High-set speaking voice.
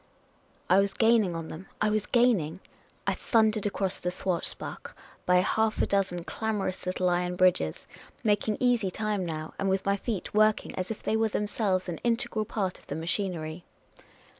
Yes: high, 195 Hz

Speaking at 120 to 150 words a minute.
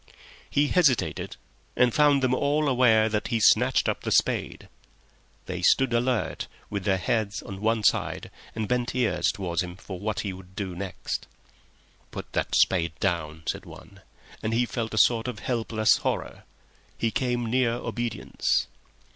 No: average, 165 wpm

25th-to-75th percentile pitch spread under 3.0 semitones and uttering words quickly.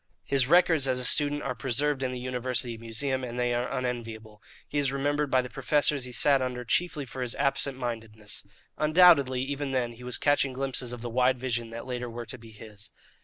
Yes: narrow, 2.4 semitones; fast, 210 wpm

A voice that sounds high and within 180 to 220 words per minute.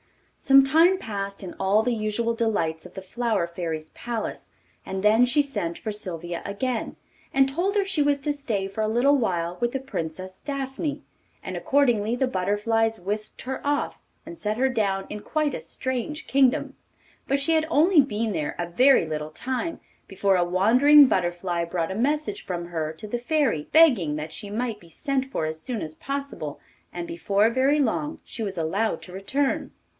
Yes: high, 225 Hz; average, 185 wpm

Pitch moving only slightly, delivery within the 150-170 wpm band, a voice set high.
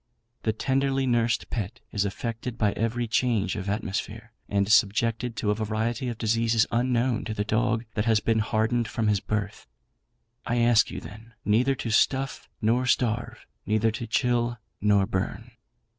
No: narrow, 2.0 semitones; average, 160 wpm; low, 115 Hz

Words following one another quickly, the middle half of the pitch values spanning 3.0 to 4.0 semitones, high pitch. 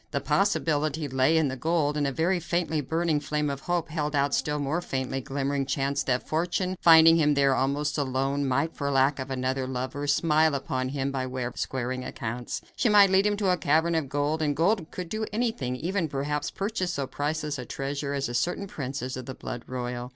No: fast, 215 wpm; average, 3.5 semitones; medium, 145 Hz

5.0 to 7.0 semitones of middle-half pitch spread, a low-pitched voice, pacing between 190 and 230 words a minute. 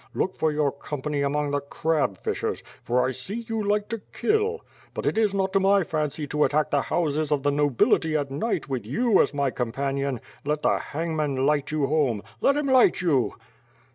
No: wide, 5.4 semitones; medium, 150 Hz; average, 200 wpm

